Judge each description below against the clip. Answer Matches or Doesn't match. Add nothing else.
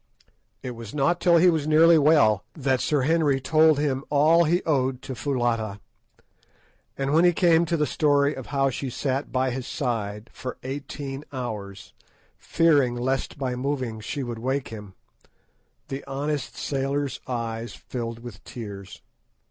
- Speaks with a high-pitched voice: Doesn't match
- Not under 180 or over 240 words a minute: Doesn't match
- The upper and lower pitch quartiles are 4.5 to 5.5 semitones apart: Doesn't match